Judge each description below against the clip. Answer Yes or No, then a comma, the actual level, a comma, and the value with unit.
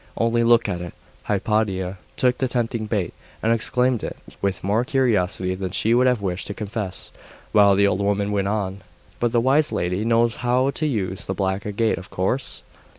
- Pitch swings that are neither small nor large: Yes, average, 3.6 semitones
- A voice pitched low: Yes, low, 105 Hz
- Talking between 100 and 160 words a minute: No, average, 190 wpm